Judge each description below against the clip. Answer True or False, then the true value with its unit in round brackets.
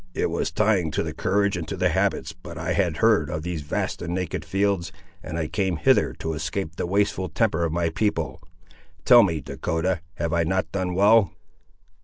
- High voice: False (90 Hz)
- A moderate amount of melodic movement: True (3.3 semitones)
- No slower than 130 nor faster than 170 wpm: False (200 wpm)